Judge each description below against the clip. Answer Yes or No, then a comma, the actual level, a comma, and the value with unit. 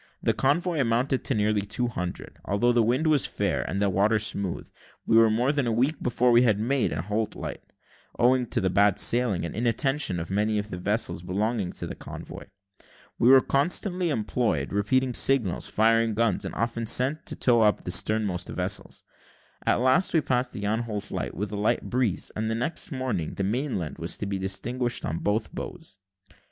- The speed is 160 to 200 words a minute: Yes, average, 190 wpm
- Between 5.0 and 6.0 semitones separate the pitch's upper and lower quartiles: No, average, 3.8 semitones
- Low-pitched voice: Yes, low, 115 Hz